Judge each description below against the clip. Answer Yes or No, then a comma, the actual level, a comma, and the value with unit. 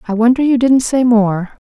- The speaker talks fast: Yes, fast, 215 wpm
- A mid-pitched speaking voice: No, high, 235 Hz